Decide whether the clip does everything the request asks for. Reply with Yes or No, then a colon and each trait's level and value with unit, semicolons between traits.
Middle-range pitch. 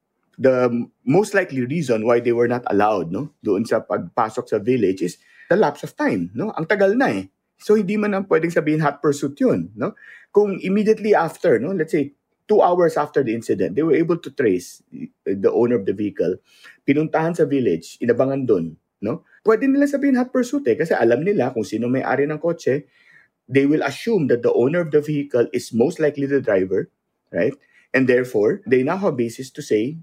Yes: medium, 145 Hz